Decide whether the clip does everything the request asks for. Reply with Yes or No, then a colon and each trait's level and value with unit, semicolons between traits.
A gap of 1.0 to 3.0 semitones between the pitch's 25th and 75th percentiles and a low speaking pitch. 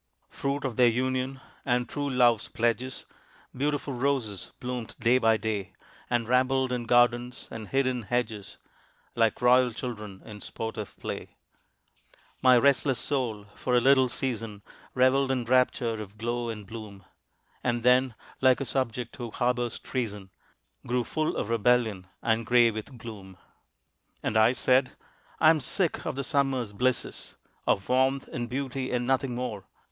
Yes: narrow, 2.5 semitones; low, 125 Hz